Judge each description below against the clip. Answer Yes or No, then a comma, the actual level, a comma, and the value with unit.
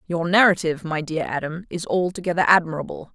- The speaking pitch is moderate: Yes, medium, 170 Hz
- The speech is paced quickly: No, average, 150 wpm